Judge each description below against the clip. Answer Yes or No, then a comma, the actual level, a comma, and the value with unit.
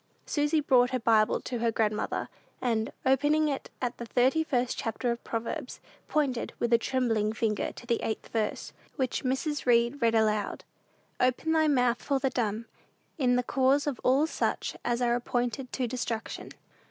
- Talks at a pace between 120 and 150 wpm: No, average, 170 wpm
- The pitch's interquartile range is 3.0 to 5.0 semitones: No, narrow, 2.5 semitones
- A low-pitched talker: No, high, 245 Hz